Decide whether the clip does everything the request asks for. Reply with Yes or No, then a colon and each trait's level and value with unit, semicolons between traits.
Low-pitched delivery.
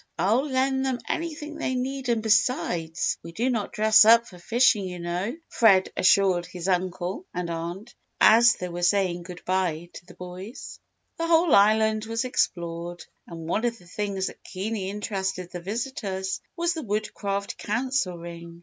No: high, 200 Hz